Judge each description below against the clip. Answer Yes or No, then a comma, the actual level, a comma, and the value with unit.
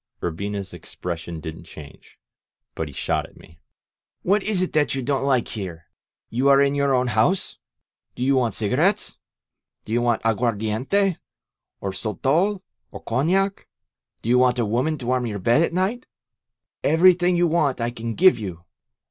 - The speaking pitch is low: Yes, low, 125 Hz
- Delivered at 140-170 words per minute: Yes, average, 165 wpm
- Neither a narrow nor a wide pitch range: No, wide, 7.2 semitones